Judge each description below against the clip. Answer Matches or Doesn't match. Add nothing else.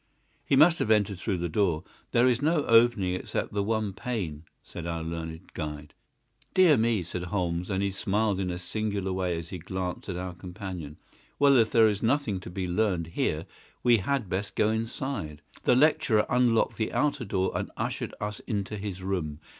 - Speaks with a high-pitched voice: Doesn't match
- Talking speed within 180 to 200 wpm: Matches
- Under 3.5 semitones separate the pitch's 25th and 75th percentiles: Doesn't match